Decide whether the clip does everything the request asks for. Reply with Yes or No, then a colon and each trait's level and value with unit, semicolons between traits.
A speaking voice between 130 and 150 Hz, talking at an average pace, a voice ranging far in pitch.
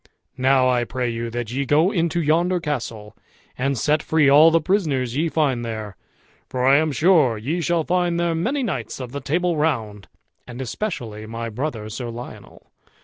Yes: medium, 140 Hz; average, 180 wpm; wide, 5.7 semitones